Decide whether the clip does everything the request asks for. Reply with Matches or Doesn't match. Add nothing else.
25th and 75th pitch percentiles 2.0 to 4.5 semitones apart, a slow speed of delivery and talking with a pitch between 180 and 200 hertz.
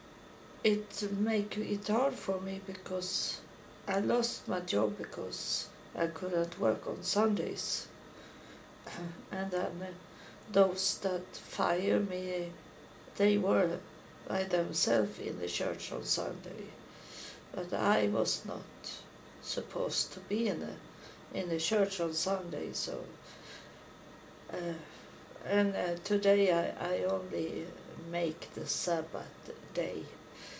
Matches